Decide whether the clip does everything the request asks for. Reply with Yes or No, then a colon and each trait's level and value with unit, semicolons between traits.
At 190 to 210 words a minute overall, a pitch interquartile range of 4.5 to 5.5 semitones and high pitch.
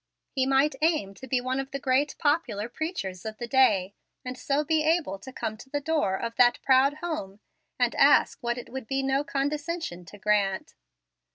Yes: average, 195 wpm; average, 5.1 semitones; very high, 265 Hz